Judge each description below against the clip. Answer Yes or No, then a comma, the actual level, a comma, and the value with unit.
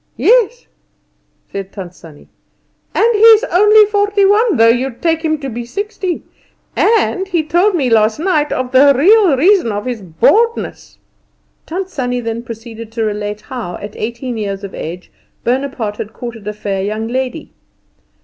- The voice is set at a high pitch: Yes, very high, 255 Hz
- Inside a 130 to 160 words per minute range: Yes, average, 155 wpm